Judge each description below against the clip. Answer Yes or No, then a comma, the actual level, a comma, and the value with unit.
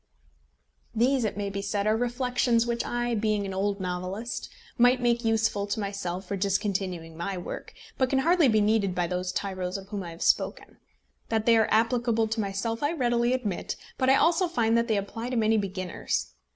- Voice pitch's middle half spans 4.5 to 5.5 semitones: No, average, 3.5 semitones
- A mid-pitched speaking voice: No, high, 215 Hz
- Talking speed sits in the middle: Yes, average, 195 wpm